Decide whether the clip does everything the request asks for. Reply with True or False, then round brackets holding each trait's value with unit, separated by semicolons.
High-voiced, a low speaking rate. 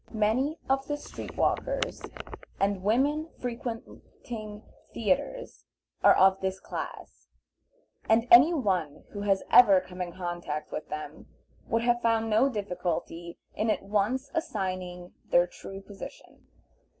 True (210 Hz; 125 wpm)